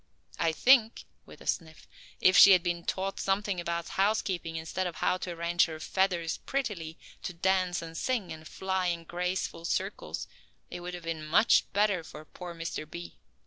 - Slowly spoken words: No, average, 180 wpm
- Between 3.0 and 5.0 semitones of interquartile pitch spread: No, narrow, 2.4 semitones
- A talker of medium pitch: Yes, medium, 175 Hz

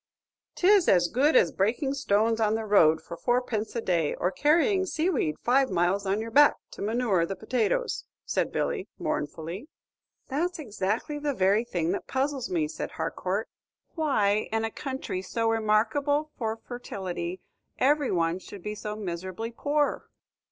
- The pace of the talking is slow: No, average, 160 wpm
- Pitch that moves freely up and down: Yes, wide, 6.7 semitones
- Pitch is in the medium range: No, high, 225 Hz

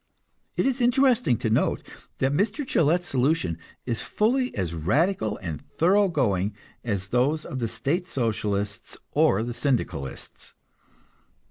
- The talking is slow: Yes, slow, 130 wpm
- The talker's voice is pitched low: Yes, low, 130 Hz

